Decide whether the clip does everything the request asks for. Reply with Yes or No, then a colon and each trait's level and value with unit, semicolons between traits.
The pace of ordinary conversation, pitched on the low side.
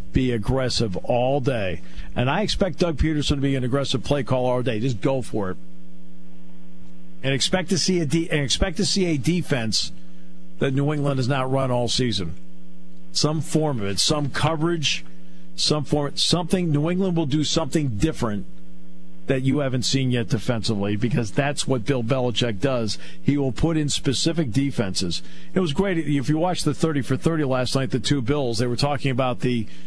Yes: average, 190 wpm; low, 130 Hz